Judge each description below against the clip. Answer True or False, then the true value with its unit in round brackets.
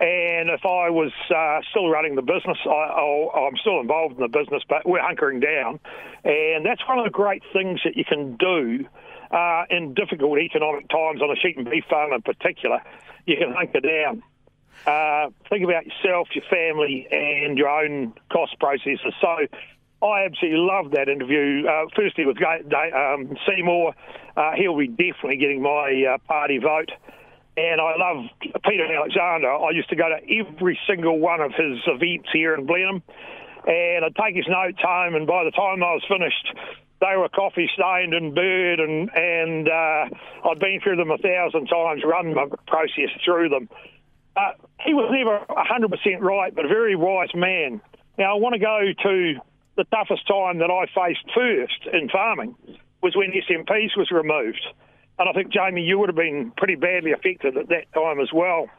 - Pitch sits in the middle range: True (175 Hz)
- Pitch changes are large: False (3.7 semitones)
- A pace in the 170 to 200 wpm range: True (185 wpm)